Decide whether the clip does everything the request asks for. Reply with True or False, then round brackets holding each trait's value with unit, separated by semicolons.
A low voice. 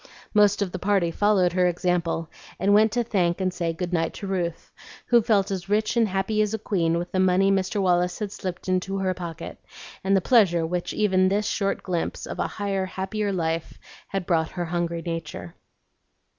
False (185 Hz)